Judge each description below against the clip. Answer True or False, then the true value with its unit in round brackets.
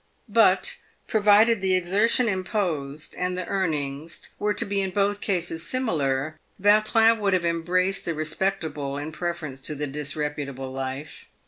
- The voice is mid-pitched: True (175 Hz)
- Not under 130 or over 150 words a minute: True (140 wpm)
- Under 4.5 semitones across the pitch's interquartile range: False (5.1 semitones)